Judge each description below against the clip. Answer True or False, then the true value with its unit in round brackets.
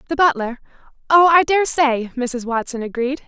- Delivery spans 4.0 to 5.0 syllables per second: True (4.7 syllables/s)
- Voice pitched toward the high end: True (275 Hz)